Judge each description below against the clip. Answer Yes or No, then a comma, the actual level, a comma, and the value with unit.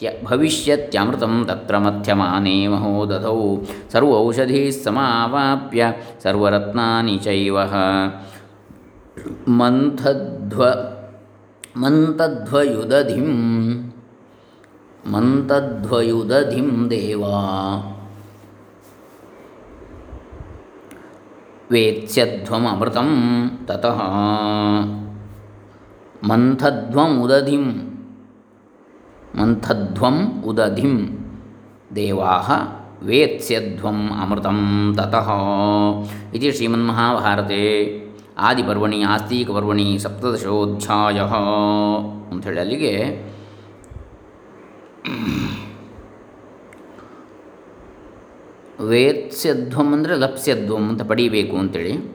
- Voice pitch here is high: No, low, 105 Hz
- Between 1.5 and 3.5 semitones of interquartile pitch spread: Yes, average, 2.9 semitones